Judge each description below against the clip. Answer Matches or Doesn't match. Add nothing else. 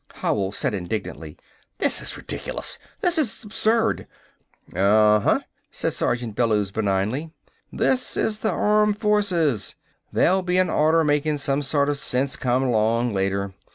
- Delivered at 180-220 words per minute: Doesn't match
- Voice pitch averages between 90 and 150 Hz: Matches